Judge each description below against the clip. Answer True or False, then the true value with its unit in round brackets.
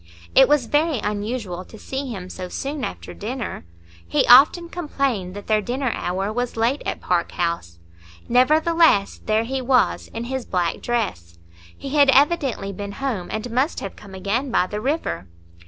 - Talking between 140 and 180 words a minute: True (170 wpm)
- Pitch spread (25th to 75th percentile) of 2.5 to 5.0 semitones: False (5.5 semitones)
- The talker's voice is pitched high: True (235 Hz)